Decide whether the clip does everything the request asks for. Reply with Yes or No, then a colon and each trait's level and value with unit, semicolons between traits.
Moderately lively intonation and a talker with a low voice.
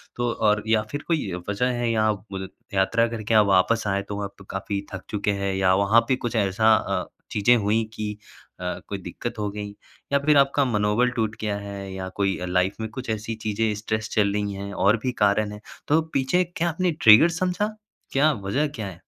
Yes: average, 3.1 semitones; low, 105 Hz